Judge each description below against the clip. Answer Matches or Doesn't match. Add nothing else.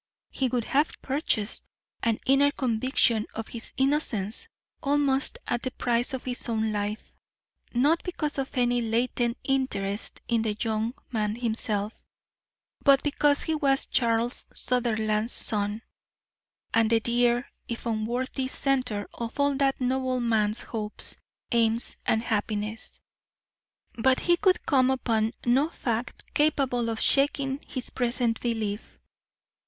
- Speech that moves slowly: Matches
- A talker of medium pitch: Doesn't match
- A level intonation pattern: Doesn't match